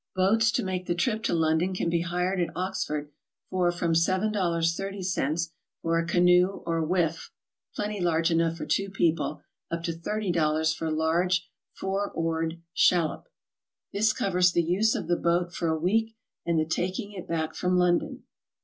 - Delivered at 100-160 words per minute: No, average, 170 wpm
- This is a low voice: No, medium, 175 Hz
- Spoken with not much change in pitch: Yes, narrow, 2.3 semitones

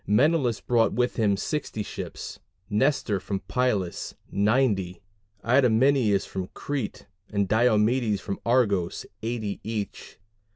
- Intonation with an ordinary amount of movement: Yes, average, 3.7 semitones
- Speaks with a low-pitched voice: Yes, low, 110 Hz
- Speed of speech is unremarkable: No, slow, 110 wpm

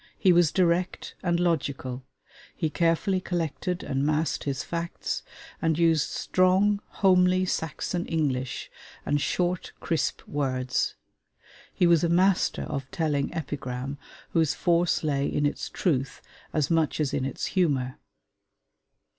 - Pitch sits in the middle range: Yes, medium, 160 Hz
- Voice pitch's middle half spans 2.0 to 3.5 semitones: No, average, 3.9 semitones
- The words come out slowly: Yes, slow, 130 wpm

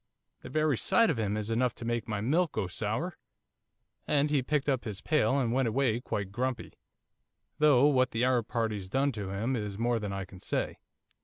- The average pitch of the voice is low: Yes, low, 120 Hz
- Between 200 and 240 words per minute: Yes, fast, 205 wpm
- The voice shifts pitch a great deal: No, average, 4.3 semitones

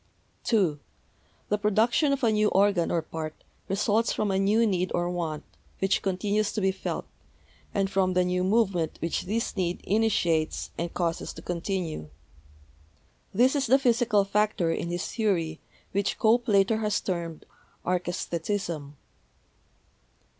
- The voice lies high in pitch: Yes, high, 195 Hz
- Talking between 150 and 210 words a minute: No, average, 140 wpm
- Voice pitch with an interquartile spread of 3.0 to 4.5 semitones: Yes, average, 3.6 semitones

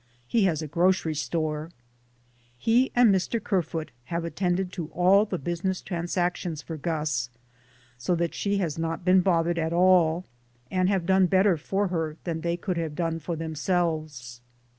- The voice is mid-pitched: Yes, medium, 170 Hz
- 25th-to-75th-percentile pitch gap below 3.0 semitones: Yes, narrow, 2.6 semitones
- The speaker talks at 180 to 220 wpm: No, average, 160 wpm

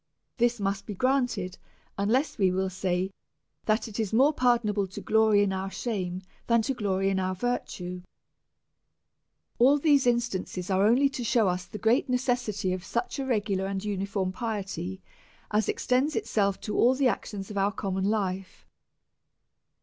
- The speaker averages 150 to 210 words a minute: Yes, average, 165 wpm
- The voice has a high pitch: Yes, high, 205 Hz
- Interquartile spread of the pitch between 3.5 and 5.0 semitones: Yes, average, 4.0 semitones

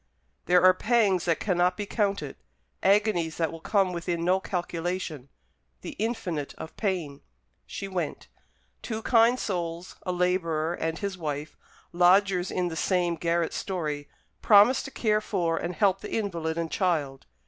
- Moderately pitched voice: Yes, medium, 180 Hz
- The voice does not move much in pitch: No, average, 3.1 semitones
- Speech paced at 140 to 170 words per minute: Yes, average, 150 wpm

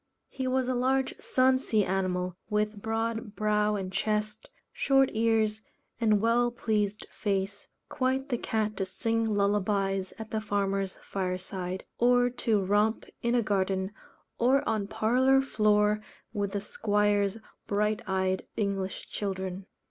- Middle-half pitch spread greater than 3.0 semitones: No, narrow, 2.6 semitones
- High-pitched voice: Yes, high, 210 Hz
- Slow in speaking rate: Yes, slow, 130 wpm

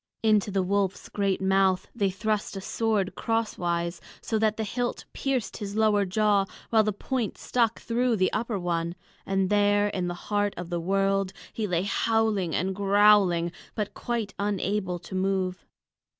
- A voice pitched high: Yes, high, 200 Hz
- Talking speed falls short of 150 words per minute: No, average, 165 wpm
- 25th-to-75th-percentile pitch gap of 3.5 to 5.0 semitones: No, narrow, 2.4 semitones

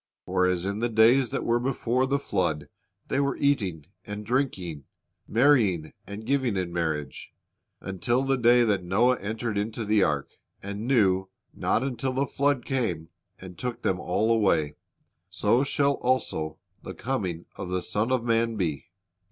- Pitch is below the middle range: Yes, low, 110 Hz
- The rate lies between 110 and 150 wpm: No, average, 160 wpm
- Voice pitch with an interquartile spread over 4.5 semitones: Yes, wide, 5.6 semitones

